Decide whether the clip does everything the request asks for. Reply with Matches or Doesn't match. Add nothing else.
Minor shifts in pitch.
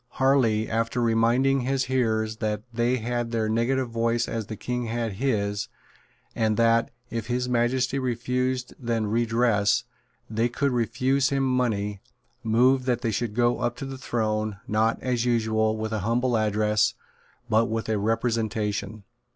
Matches